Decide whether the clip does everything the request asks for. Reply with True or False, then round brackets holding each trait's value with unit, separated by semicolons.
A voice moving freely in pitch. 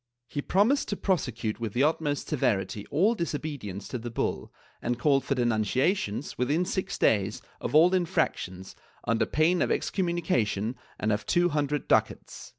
True (7.6 semitones)